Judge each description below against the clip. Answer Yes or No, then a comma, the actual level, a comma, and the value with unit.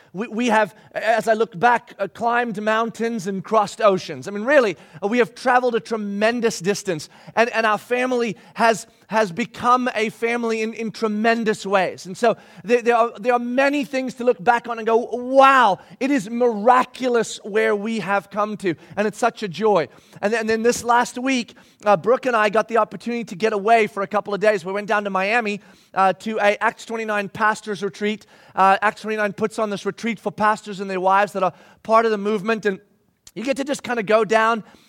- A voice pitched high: Yes, high, 220 Hz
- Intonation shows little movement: Yes, narrow, 2.3 semitones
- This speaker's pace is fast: Yes, fast, 210 wpm